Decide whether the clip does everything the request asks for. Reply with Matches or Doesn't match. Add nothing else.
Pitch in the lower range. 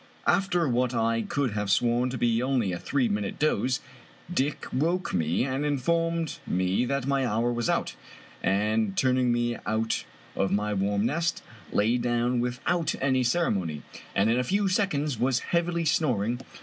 Matches